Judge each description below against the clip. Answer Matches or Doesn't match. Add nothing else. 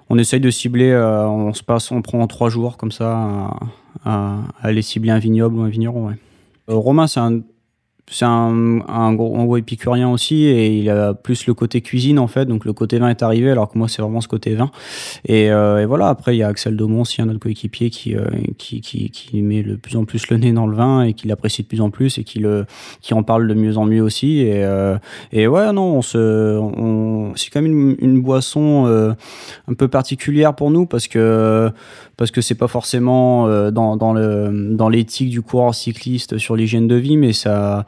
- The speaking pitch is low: Matches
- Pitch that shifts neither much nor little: Doesn't match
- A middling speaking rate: Doesn't match